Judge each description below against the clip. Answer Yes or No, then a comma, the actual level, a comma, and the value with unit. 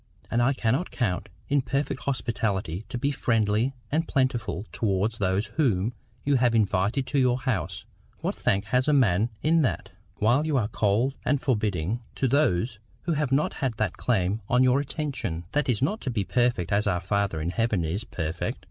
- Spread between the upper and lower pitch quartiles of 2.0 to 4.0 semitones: No, average, 5.2 semitones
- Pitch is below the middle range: Yes, low, 115 Hz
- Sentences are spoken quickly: No, average, 175 wpm